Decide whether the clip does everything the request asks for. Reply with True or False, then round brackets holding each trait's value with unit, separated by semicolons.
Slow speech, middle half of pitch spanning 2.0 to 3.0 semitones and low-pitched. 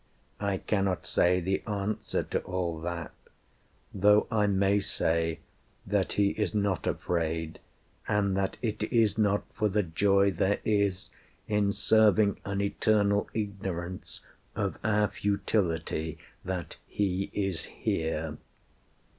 True (120 wpm; 2.4 semitones; 100 Hz)